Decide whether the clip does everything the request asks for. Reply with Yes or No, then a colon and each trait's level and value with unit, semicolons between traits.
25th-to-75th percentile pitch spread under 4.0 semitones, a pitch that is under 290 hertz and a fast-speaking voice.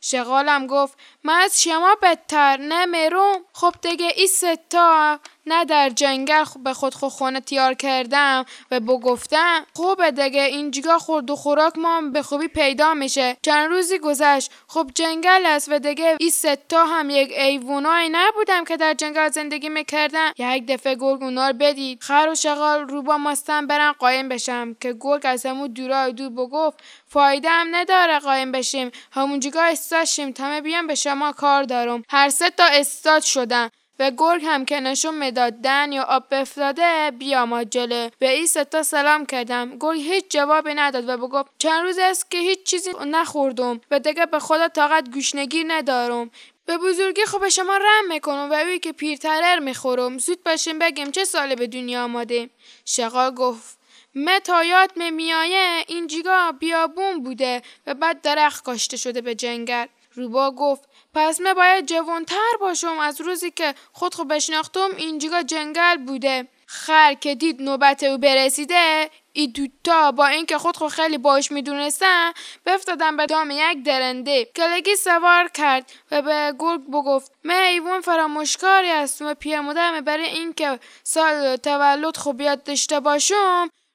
No: average, 3.5 semitones; very high, 300 Hz; fast, 160 wpm